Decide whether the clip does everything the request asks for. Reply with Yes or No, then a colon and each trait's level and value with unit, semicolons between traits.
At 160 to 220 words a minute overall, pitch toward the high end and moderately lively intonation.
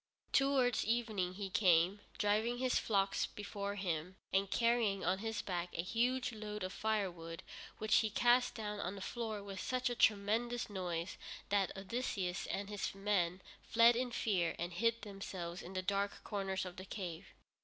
Yes: average, 165 wpm; high, 200 Hz; average, 3.4 semitones